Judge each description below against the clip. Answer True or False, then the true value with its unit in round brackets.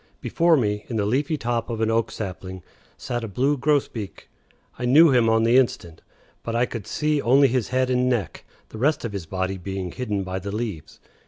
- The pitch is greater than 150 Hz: False (115 Hz)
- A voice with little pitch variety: False (4.4 semitones)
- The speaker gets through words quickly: True (210 wpm)